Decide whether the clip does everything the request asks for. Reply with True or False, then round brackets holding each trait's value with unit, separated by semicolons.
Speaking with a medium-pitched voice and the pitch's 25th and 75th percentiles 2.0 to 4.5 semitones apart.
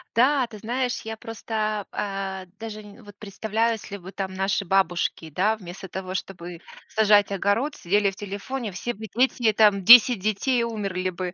False (205 Hz; 2.7 semitones)